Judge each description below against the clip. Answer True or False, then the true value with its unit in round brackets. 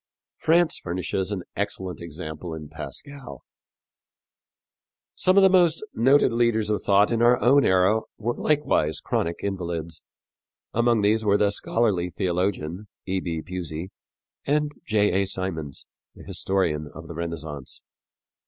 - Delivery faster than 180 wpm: False (135 wpm)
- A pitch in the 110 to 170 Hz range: False (95 Hz)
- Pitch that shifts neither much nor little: False (5.7 semitones)